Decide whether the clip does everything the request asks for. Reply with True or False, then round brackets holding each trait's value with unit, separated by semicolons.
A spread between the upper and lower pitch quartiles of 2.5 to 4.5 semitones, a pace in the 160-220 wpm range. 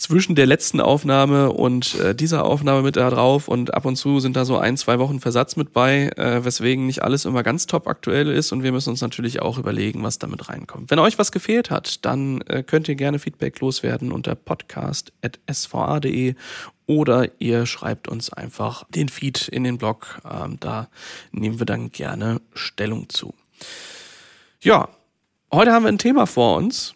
True (3.1 semitones; 185 wpm)